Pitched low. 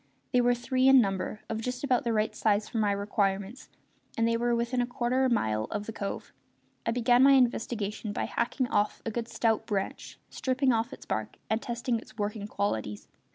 No: high, 230 Hz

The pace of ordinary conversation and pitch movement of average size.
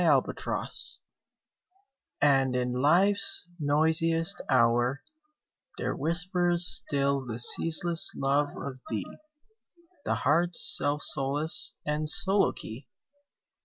No: slow, 90 wpm; average, 4.0 semitones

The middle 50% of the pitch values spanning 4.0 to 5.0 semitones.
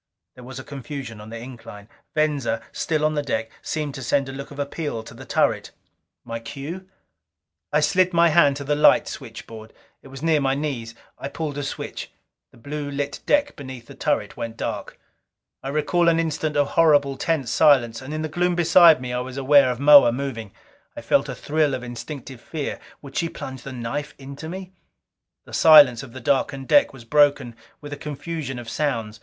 No: average, 3.5 semitones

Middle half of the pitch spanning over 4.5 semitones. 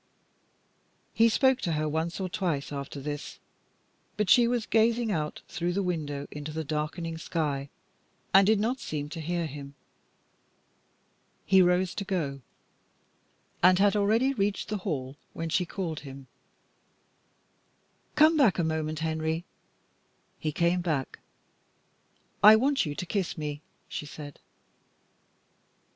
Yes: average, 4.9 semitones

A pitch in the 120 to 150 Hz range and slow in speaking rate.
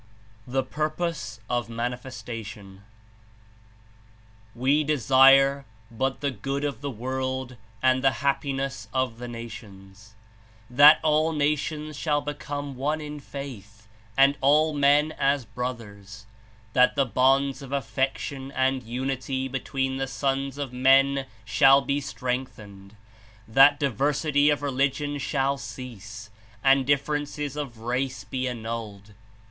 Yes: low, 135 Hz; slow, 120 wpm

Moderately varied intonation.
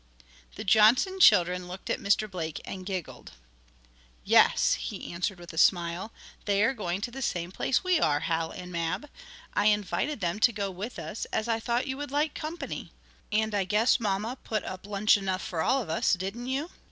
Yes: average, 4.8 semitones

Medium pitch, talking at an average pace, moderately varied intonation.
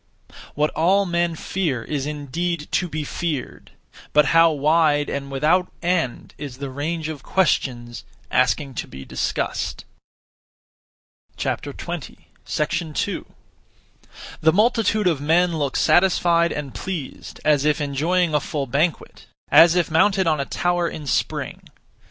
No: medium, 155 Hz; slow, 130 wpm; average, 3.3 semitones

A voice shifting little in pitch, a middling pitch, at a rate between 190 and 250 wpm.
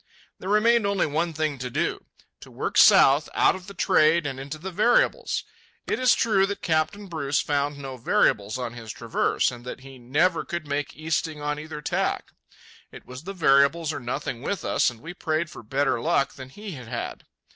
No: average, 4.4 semitones; medium, 150 Hz; average, 195 wpm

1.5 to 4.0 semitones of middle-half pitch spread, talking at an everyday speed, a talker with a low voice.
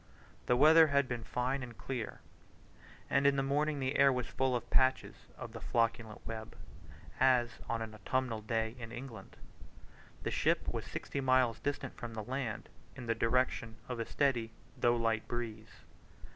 Yes: narrow, 2.6 semitones; average, 170 wpm; low, 120 Hz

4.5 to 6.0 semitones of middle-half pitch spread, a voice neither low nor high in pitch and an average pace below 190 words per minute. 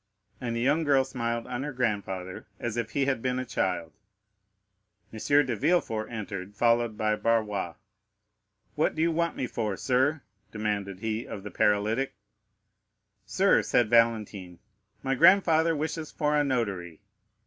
No: average, 4.8 semitones; low, 115 Hz; average, 150 wpm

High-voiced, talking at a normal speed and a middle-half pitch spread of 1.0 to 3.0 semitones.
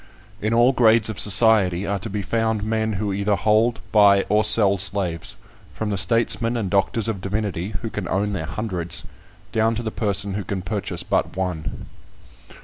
No: low, 105 Hz; average, 180 wpm; narrow, 2.5 semitones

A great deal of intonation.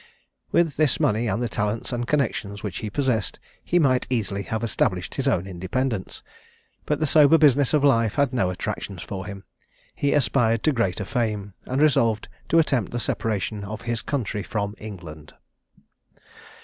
No: average, 4.9 semitones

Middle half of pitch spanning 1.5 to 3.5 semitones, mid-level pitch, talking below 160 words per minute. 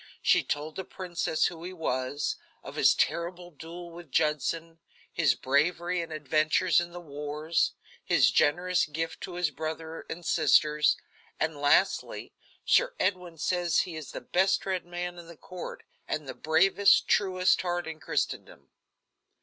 Yes: narrow, 2.5 semitones; medium, 165 Hz; average, 150 wpm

